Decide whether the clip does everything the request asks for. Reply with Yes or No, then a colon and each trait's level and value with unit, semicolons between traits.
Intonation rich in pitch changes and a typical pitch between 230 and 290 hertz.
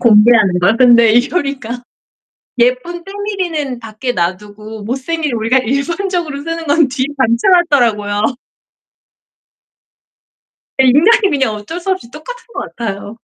Yes: wide, 6.6 semitones; very high, 255 Hz